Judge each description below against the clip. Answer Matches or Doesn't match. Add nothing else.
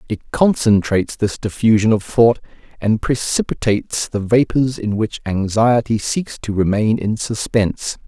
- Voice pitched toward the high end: Doesn't match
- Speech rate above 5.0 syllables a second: Doesn't match